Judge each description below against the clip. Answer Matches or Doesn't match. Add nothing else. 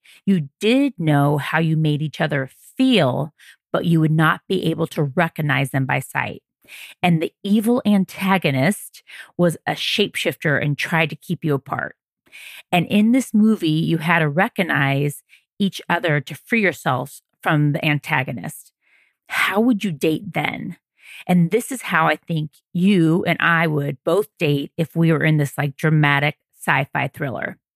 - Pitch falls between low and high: Matches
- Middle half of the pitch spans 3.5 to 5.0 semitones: Matches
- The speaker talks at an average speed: Matches